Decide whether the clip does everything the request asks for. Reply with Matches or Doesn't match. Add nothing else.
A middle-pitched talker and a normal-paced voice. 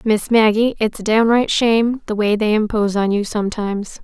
Doesn't match